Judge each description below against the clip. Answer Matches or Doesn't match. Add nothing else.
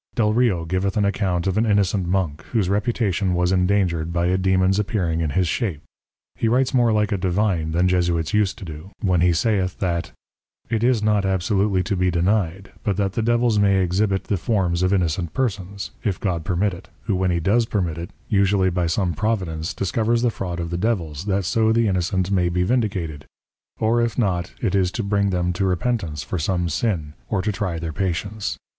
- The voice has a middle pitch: Doesn't match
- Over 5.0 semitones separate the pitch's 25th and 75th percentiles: Doesn't match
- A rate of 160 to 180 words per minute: Doesn't match